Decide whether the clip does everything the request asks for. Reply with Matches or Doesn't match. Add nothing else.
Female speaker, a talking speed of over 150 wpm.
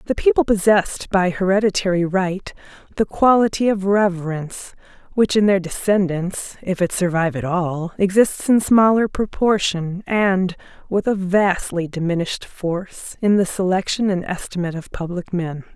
Doesn't match